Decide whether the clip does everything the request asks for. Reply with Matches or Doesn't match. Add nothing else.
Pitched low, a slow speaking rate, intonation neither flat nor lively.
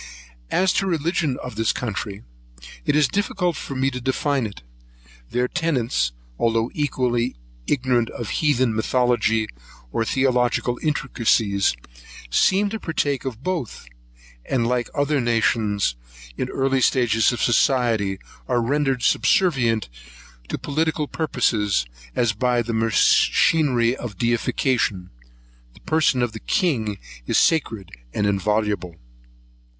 Matches